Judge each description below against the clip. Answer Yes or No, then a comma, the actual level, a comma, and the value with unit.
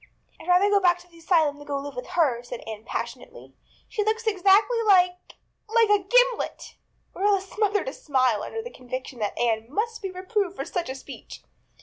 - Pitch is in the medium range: No, very high, 360 Hz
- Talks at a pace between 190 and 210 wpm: Yes, fast, 205 wpm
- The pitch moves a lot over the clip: Yes, wide, 7.1 semitones